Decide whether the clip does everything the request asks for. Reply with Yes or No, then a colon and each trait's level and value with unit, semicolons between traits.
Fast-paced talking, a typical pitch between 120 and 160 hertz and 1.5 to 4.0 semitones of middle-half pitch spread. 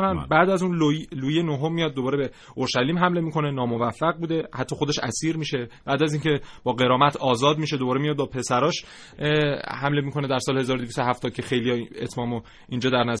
Yes: fast, 180 wpm; medium, 140 Hz; average, 3.6 semitones